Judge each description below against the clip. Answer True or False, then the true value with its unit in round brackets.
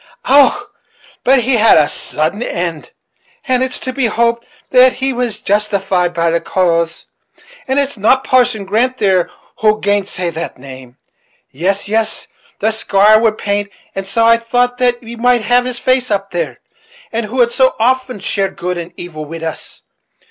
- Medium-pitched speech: False (215 Hz)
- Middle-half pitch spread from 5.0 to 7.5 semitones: True (5.4 semitones)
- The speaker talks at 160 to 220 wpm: True (170 wpm)